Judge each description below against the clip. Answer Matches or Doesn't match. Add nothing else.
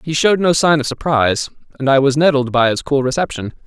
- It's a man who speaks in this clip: Matches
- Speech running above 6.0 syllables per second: Matches